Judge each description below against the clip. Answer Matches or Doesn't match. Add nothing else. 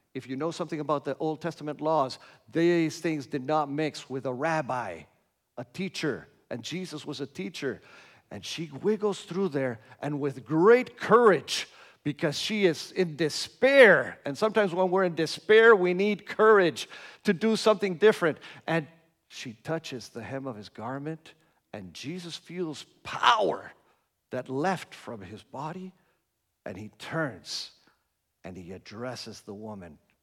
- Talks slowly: Doesn't match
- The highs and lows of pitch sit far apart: Matches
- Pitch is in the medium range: Matches